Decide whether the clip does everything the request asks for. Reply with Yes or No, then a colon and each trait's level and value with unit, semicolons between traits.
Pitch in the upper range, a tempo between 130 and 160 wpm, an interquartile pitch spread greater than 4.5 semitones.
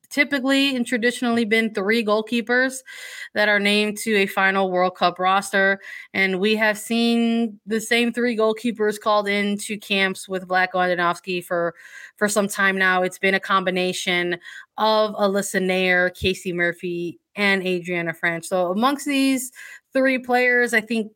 No: high, 205 Hz; average, 150 wpm; average, 4.0 semitones